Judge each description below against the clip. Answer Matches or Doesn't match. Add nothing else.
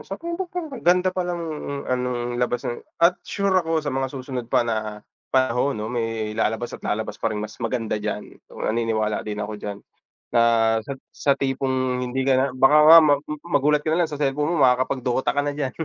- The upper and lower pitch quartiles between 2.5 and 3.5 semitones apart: Doesn't match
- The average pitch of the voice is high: Doesn't match